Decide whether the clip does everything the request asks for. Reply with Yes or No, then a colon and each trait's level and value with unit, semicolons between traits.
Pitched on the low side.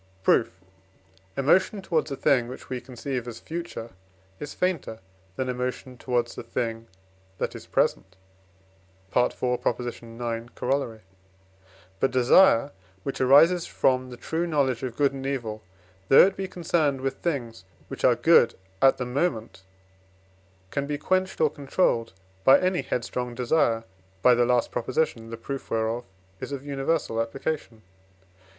Yes: low, 130 Hz